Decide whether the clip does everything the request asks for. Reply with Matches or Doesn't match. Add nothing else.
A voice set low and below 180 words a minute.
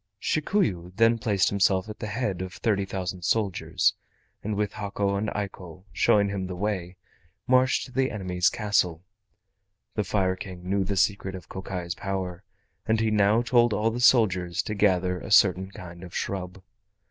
Matches